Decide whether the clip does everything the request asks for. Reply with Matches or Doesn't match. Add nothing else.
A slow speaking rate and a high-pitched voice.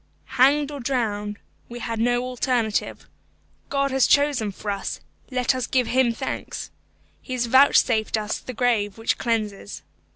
Doesn't match